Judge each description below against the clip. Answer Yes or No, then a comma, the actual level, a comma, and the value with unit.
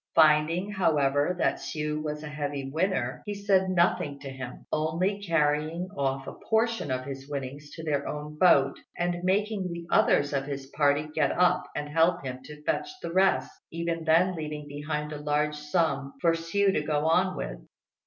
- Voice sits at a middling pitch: Yes, medium, 150 Hz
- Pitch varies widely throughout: No, average, 3.4 semitones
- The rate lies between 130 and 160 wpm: No, average, 180 wpm